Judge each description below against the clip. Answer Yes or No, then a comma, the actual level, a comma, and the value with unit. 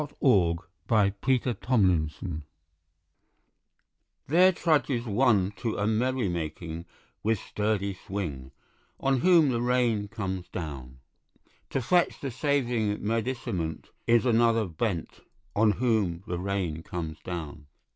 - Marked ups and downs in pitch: Yes, wide, 5.8 semitones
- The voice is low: Yes, low, 105 Hz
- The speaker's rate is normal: No, slow, 120 wpm